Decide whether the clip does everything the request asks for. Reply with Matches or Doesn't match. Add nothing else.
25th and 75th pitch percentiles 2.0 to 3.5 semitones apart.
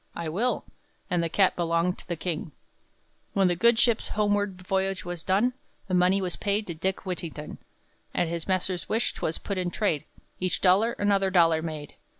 Matches